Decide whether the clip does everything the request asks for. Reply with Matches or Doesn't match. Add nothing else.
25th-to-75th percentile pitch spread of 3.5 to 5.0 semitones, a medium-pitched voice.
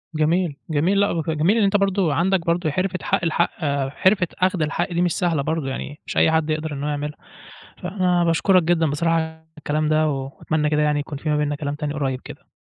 Doesn't match